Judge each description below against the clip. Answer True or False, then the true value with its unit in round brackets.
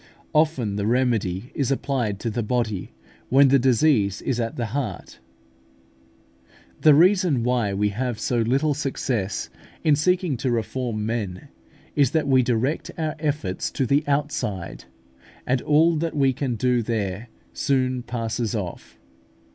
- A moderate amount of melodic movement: True (4.2 semitones)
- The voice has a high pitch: False (125 Hz)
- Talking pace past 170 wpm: False (145 wpm)